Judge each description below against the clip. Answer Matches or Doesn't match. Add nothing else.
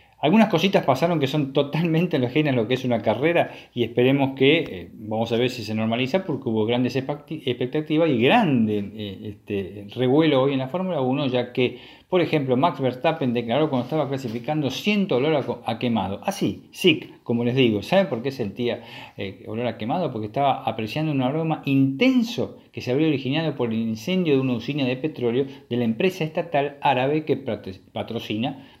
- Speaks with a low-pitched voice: Matches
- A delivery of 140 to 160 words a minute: Doesn't match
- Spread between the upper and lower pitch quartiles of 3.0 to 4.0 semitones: Doesn't match